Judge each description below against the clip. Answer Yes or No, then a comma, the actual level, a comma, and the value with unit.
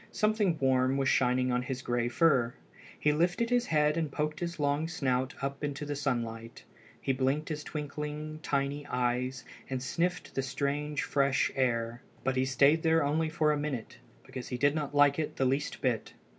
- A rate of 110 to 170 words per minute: No, average, 185 wpm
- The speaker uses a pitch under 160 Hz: Yes, medium, 140 Hz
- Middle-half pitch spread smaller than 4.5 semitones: Yes, average, 2.9 semitones